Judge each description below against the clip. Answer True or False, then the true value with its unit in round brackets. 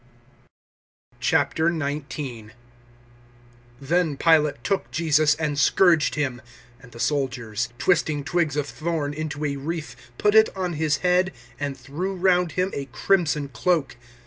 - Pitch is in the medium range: True (150 Hz)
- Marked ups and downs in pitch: False (3.6 semitones)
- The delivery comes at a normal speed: False (130 wpm)